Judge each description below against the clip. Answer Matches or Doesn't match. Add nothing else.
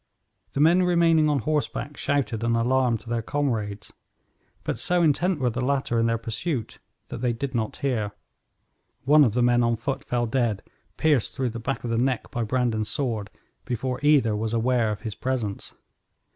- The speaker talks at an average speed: Matches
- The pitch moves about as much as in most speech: Matches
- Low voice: Matches